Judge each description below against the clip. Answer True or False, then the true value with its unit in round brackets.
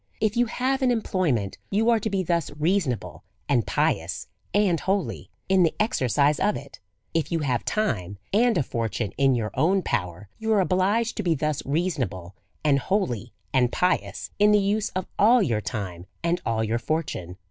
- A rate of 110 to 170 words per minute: False (180 wpm)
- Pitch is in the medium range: True (160 Hz)